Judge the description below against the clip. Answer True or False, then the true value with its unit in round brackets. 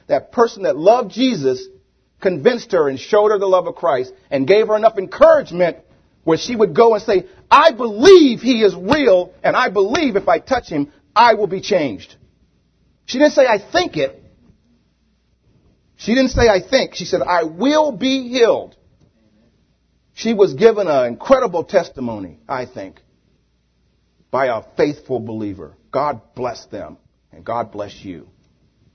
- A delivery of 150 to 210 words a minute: True (160 wpm)